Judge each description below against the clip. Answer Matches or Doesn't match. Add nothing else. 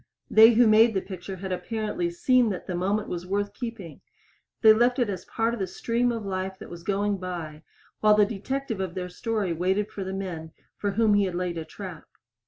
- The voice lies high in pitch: Matches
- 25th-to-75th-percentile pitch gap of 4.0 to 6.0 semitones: Doesn't match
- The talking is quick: Matches